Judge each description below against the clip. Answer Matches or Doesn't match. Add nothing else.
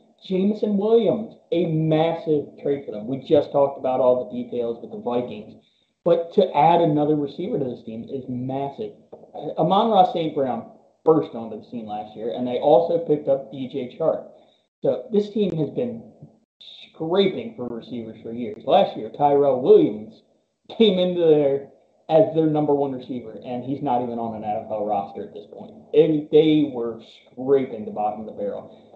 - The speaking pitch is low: Doesn't match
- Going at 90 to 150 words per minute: Doesn't match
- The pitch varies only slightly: Doesn't match